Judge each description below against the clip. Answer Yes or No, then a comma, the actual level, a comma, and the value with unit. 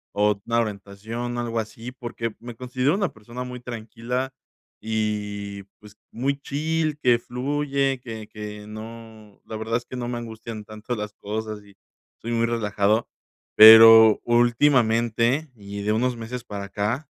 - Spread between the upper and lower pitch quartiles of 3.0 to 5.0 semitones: No, narrow, 2.5 semitones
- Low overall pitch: Yes, low, 115 Hz